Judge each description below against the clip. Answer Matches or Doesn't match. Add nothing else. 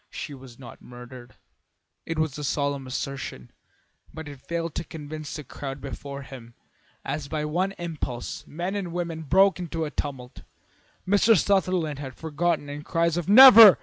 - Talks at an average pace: Matches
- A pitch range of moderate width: Matches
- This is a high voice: Doesn't match